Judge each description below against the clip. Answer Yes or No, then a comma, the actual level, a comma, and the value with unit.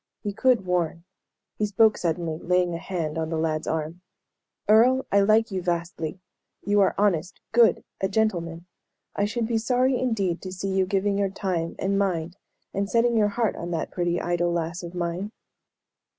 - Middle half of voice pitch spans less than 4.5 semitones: Yes, average, 3.6 semitones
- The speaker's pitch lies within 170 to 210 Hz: Yes, medium, 185 Hz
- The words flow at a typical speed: Yes, average, 180 wpm